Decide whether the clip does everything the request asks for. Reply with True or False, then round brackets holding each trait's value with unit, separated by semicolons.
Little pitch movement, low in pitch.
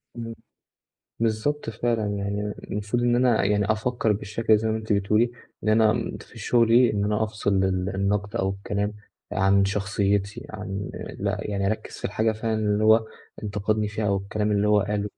True (1.5 semitones; 105 Hz)